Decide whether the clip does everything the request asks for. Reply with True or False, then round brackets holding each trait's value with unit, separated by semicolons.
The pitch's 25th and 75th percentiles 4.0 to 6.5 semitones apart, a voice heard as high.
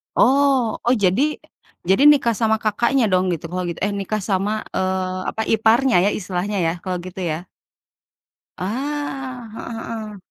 True (4.7 semitones; 215 Hz)